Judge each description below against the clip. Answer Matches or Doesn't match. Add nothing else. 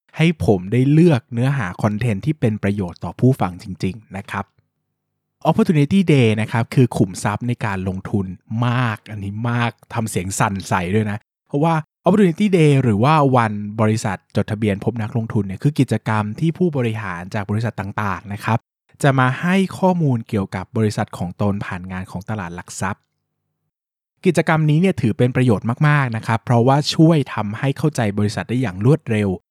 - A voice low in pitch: Matches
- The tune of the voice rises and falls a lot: Doesn't match